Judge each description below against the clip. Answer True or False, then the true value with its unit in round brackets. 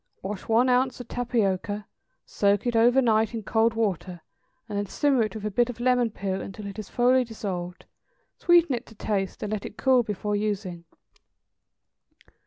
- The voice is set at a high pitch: True (220 Hz)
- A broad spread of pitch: False (3.3 semitones)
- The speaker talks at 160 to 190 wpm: True (185 wpm)